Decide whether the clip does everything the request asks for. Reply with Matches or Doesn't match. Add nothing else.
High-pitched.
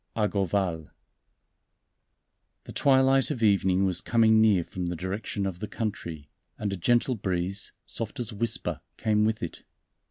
Doesn't match